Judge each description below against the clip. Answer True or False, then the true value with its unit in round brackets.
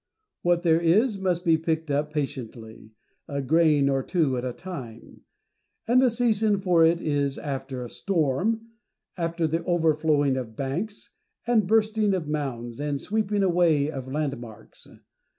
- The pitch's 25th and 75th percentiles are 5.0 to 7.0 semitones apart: True (5.4 semitones)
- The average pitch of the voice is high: False (160 Hz)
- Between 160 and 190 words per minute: False (150 wpm)